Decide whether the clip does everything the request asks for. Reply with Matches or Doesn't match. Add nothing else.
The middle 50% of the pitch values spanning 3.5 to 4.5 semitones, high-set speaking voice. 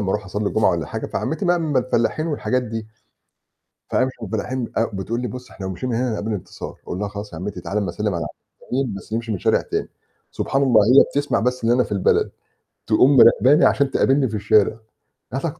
Doesn't match